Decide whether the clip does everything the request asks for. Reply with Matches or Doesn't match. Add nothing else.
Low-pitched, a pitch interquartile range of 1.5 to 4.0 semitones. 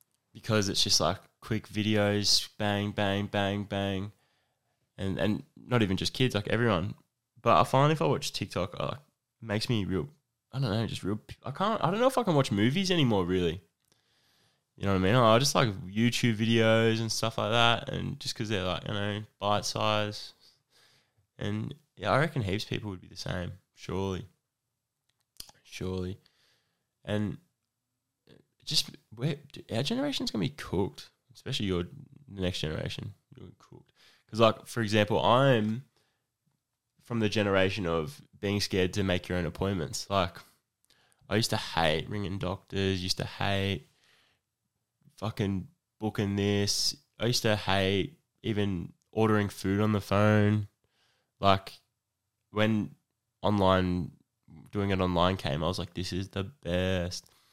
Matches